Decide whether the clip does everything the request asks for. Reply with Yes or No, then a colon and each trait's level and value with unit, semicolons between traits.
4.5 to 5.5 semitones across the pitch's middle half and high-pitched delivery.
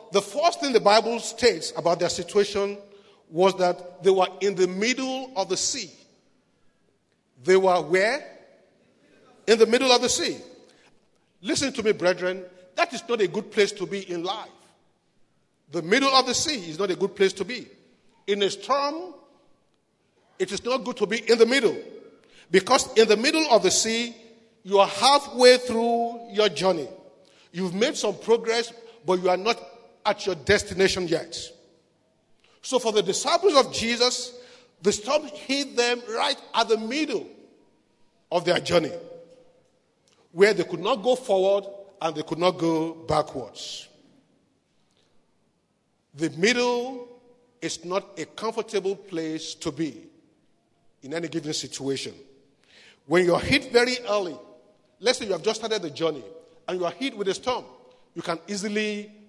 Yes: average, 5.1 semitones; high, 210 Hz